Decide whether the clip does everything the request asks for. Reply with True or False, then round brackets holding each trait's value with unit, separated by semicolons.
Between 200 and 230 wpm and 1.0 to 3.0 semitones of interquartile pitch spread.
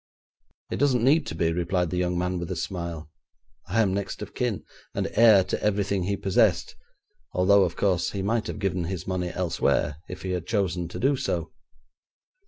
False (190 wpm; 2.5 semitones)